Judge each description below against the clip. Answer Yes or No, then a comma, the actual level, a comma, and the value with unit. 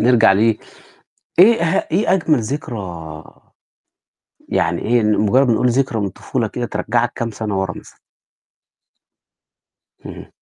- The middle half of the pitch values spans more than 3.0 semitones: Yes, average, 4.6 semitones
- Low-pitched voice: Yes, low, 115 Hz